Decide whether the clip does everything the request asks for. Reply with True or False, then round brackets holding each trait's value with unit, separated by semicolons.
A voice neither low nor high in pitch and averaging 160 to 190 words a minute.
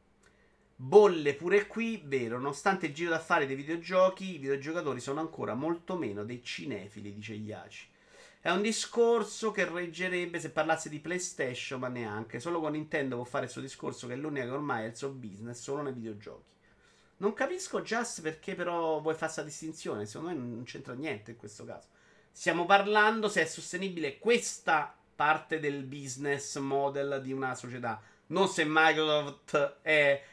True (155 Hz; 170 wpm)